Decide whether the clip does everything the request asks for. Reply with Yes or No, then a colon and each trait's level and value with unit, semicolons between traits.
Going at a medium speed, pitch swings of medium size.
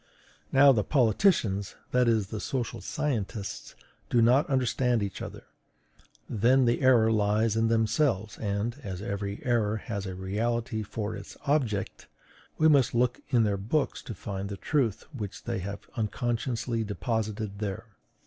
Yes: average, 150 wpm; average, 3.3 semitones